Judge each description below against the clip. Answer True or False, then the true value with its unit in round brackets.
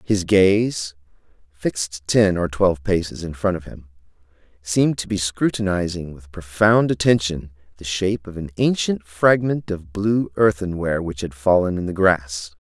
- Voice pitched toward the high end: False (90 Hz)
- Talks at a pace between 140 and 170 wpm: True (155 wpm)